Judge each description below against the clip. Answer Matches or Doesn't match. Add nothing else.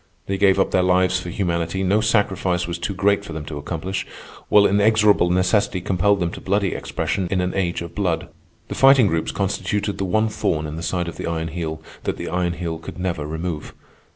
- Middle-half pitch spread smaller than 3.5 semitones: Matches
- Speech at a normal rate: Doesn't match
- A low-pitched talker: Matches